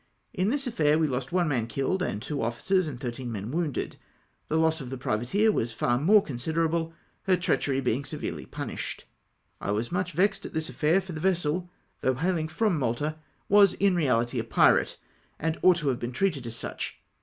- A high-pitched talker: No, medium, 155 Hz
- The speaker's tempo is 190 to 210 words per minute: Yes, average, 195 wpm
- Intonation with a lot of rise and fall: Yes, wide, 6.3 semitones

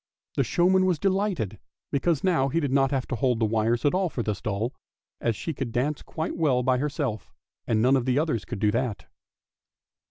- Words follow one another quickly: Yes, fast, 210 wpm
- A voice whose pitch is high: No, low, 130 Hz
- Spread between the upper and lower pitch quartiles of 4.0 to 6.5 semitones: Yes, wide, 5.4 semitones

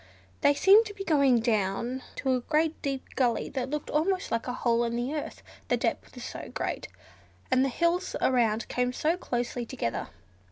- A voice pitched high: Yes, very high, 260 Hz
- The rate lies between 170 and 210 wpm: Yes, average, 190 wpm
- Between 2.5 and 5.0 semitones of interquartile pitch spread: Yes, average, 4.2 semitones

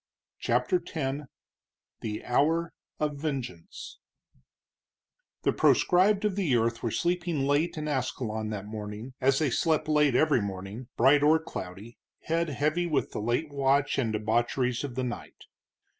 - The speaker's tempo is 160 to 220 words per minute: No, average, 145 wpm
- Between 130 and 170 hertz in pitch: Yes, low, 135 Hz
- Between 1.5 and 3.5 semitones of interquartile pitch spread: No, average, 4.9 semitones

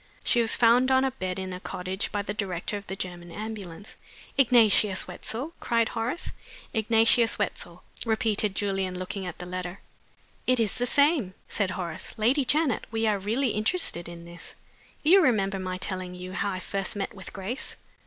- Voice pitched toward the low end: No, high, 205 Hz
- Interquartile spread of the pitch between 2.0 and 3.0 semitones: No, average, 4.1 semitones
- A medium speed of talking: Yes, average, 180 wpm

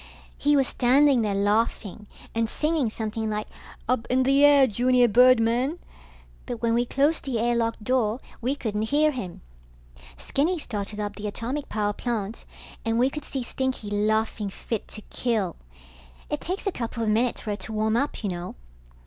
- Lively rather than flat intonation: No, average, 3.5 semitones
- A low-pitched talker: No, high, 230 Hz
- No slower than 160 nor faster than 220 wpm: Yes, average, 175 wpm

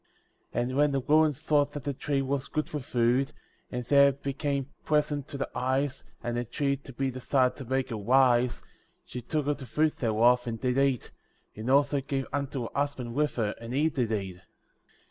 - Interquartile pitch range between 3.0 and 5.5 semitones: No, narrow, 2.6 semitones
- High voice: No, low, 135 Hz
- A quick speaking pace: Yes, fast, 210 wpm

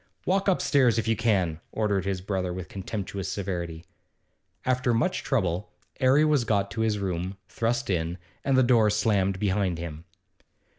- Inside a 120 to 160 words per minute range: Yes, average, 155 wpm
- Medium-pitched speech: No, low, 100 Hz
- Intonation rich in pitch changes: No, average, 4.3 semitones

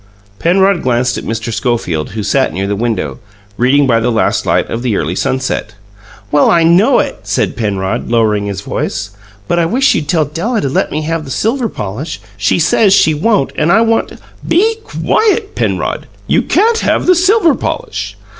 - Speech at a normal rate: Yes, average, 190 wpm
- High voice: No, medium, 150 Hz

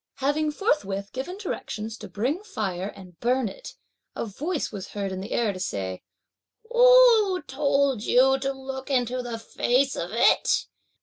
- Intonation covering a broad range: Yes, wide, 6.3 semitones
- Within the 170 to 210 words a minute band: No, average, 160 wpm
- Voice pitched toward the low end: No, very high, 255 Hz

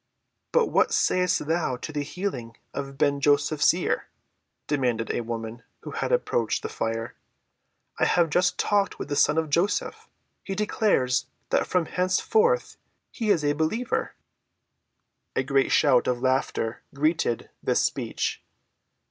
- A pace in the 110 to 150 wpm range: Yes, average, 140 wpm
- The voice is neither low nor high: Yes, medium, 145 Hz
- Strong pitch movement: Yes, wide, 6.2 semitones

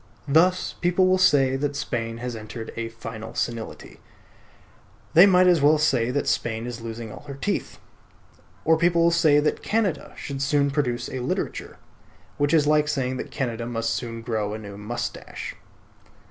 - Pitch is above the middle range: No, low, 135 Hz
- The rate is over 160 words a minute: Yes, average, 170 wpm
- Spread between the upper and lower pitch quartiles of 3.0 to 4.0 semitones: No, average, 5.1 semitones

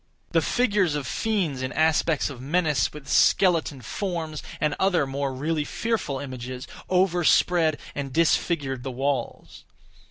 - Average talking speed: No, slow, 130 wpm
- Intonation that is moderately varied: Yes, average, 4.6 semitones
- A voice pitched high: No, medium, 150 Hz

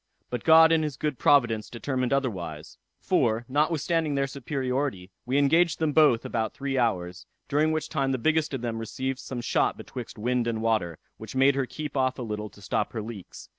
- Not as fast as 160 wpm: No, average, 195 wpm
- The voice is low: Yes, low, 130 Hz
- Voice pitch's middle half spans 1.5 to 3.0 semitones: No, average, 4.3 semitones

